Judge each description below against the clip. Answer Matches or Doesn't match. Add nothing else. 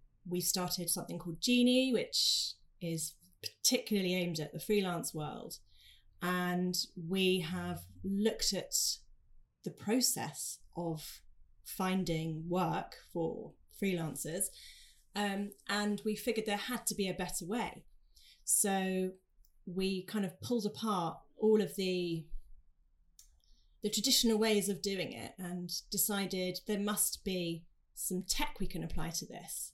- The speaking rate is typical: Doesn't match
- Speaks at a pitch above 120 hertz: Matches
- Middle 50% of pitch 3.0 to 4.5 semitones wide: Matches